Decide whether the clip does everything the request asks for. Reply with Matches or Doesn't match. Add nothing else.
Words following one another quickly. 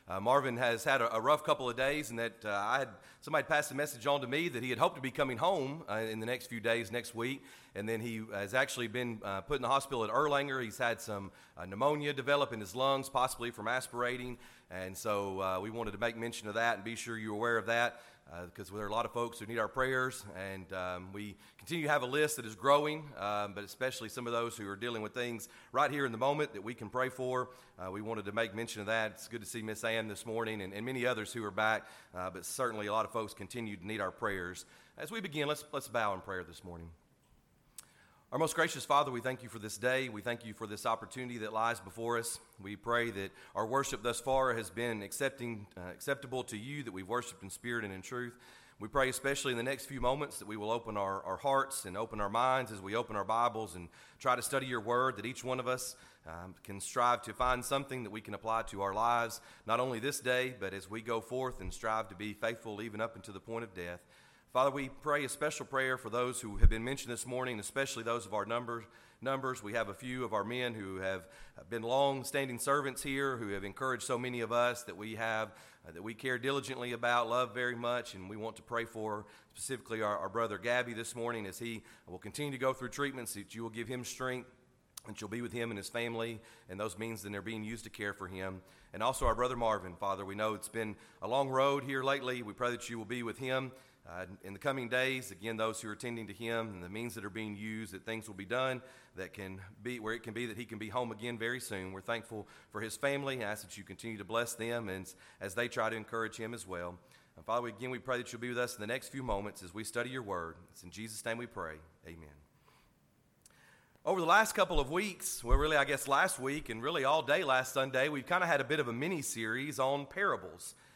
Matches